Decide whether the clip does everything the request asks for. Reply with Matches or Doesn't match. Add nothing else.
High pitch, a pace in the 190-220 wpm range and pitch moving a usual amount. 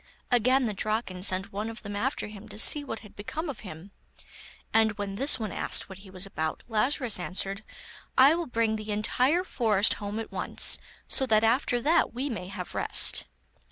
Matches